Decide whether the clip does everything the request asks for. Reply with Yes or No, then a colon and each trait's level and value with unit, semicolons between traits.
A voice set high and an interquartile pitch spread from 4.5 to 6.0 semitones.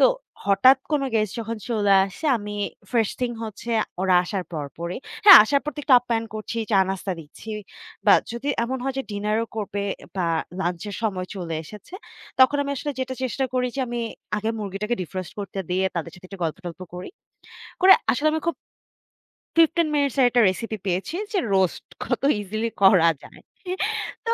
Yes: high, 215 Hz; average, 5.2 semitones